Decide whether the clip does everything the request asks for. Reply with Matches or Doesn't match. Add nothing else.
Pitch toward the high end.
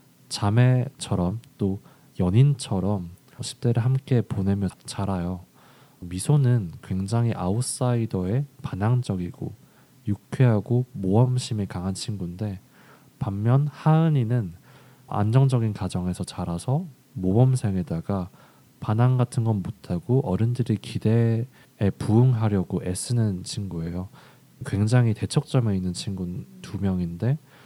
Doesn't match